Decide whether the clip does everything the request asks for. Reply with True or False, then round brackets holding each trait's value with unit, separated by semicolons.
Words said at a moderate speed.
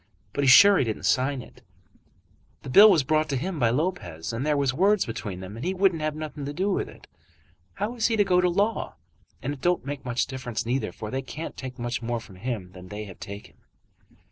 False (235 wpm)